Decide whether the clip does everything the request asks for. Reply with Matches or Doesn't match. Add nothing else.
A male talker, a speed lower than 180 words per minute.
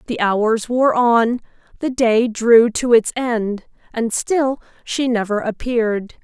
Doesn't match